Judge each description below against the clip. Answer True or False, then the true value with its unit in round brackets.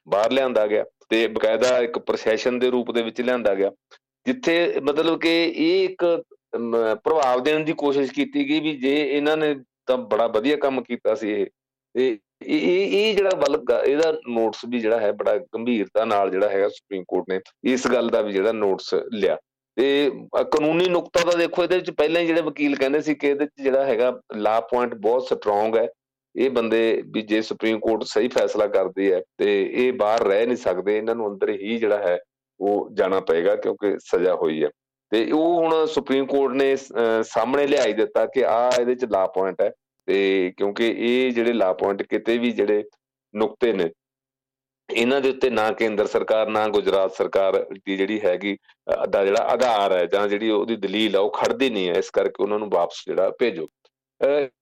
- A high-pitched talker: False (135 Hz)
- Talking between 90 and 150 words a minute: False (185 wpm)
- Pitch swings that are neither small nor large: False (6.6 semitones)